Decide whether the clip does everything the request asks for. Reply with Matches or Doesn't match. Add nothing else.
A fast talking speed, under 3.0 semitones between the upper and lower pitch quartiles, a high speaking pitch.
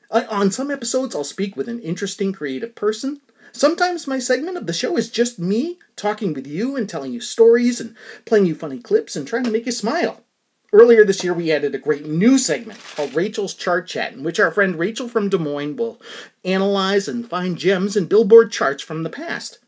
Doesn't match